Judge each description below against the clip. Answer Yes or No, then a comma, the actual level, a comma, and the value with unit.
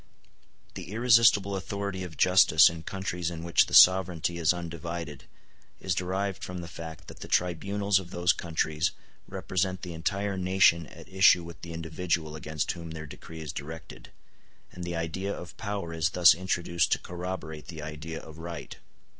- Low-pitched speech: Yes, very low, 85 Hz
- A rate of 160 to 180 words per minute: Yes, average, 165 wpm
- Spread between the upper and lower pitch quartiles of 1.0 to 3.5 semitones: Yes, narrow, 2.4 semitones